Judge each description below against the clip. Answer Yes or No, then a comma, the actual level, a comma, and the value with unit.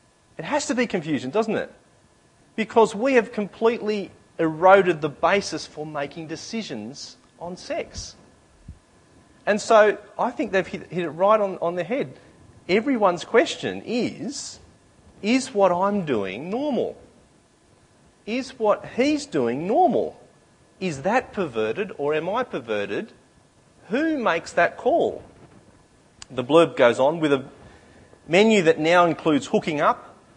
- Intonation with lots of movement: Yes, wide, 5.8 semitones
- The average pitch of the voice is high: Yes, high, 195 Hz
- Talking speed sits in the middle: No, slow, 130 wpm